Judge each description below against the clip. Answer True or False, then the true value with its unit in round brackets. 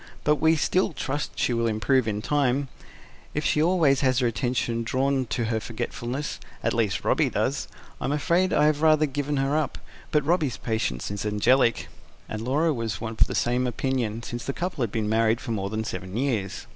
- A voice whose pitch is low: True (125 Hz)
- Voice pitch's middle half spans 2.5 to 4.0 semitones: False (4.5 semitones)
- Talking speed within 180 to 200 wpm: True (195 wpm)